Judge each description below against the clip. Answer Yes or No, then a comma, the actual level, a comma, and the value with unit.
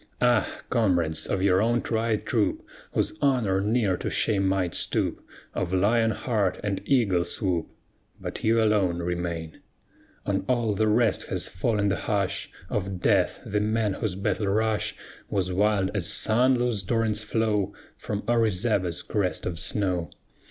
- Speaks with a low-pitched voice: Yes, low, 105 Hz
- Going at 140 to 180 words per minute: Yes, average, 150 wpm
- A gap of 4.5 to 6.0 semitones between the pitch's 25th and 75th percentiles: No, average, 3.2 semitones